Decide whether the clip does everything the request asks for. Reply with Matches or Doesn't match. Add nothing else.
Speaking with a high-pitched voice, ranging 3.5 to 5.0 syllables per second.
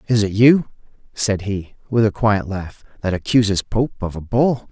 Doesn't match